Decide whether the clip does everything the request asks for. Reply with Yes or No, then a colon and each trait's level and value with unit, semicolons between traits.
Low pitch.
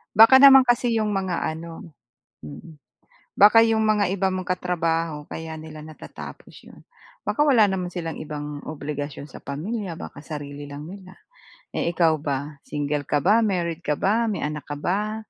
No: medium, 170 Hz